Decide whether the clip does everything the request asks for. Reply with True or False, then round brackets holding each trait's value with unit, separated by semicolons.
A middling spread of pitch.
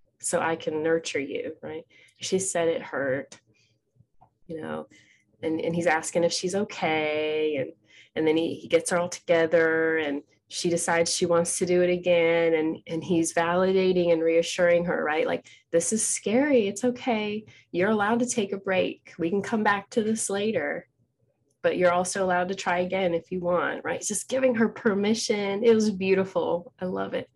True (3.5 semitones)